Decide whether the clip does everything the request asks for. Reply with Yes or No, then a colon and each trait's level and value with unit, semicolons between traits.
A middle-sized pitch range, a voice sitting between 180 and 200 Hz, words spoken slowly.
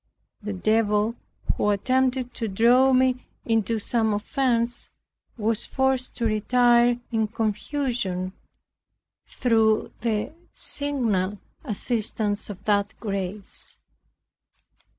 No: average, 3.0 semitones; high, 225 Hz; slow, 90 wpm